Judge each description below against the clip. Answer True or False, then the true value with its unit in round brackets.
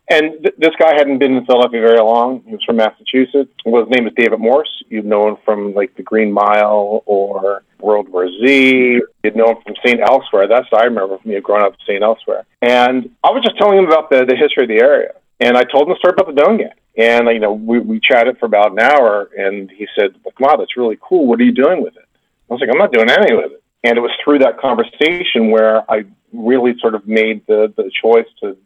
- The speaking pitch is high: False (120 Hz)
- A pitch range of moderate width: False (5.9 semitones)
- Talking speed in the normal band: False (255 wpm)